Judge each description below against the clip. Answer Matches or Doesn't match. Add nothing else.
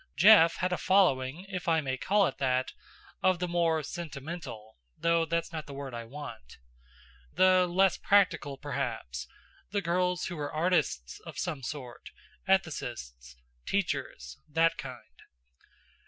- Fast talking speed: Doesn't match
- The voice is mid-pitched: Matches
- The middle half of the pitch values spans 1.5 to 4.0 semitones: Doesn't match